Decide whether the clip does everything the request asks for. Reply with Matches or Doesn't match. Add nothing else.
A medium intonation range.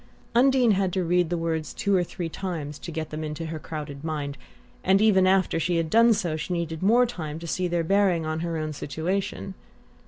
Matches